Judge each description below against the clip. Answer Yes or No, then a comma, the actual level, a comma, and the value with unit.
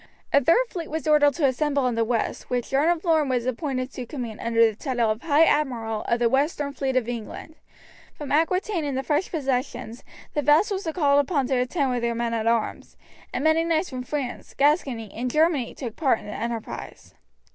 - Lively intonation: No, average, 4.3 semitones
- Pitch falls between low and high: No, very high, 270 Hz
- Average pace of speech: No, fast, 210 wpm